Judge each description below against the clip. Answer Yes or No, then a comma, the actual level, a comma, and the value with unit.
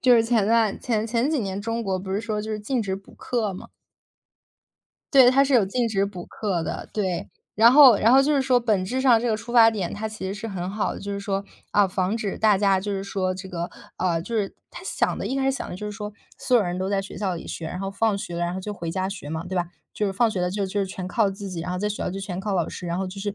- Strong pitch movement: No, average, 3.1 semitones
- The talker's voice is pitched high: Yes, high, 200 Hz